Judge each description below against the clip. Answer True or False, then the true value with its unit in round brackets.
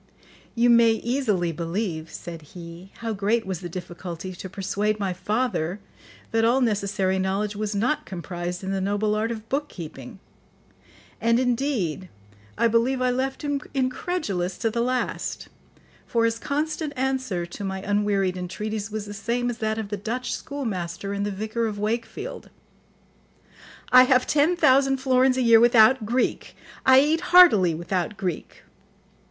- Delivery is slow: False (155 wpm)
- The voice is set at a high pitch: True (215 Hz)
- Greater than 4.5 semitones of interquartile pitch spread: True (4.9 semitones)